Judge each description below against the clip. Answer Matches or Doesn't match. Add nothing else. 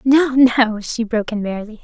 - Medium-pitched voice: Doesn't match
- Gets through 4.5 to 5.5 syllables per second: Matches